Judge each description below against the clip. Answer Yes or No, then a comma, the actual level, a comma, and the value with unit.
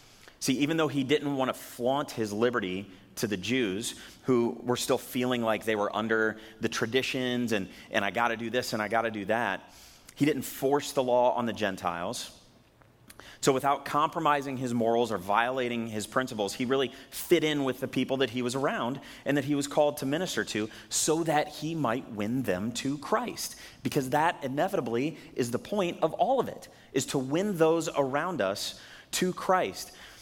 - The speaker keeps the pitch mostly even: No, average, 4.1 semitones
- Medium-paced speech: Yes, average, 195 wpm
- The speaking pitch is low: Yes, low, 130 Hz